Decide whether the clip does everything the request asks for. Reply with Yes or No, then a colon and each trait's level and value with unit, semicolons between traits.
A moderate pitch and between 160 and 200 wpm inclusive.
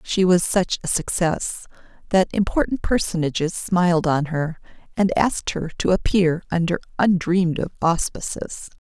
No: medium, 175 Hz; slow, 135 wpm